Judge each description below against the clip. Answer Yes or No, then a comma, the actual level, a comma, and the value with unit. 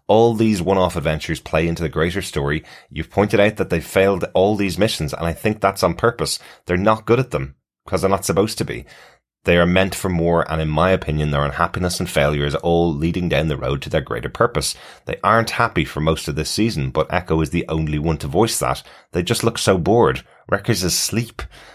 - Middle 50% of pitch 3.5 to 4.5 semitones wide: Yes, average, 3.9 semitones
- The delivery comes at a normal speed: No, fast, 235 wpm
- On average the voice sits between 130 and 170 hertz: No, very low, 85 Hz